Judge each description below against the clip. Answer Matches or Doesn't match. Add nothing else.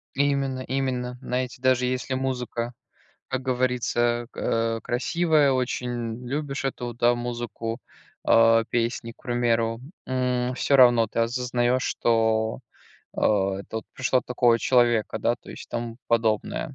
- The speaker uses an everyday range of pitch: Doesn't match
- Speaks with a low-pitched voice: Matches